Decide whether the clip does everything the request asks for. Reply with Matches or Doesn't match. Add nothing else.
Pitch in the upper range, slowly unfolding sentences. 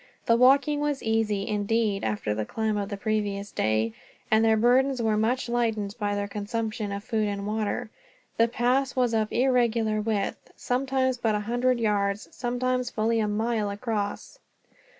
Doesn't match